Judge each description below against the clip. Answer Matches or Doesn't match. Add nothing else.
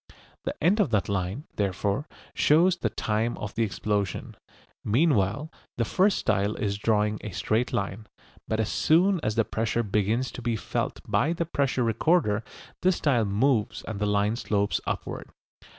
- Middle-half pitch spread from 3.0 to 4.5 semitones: Doesn't match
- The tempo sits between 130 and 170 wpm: Matches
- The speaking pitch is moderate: Doesn't match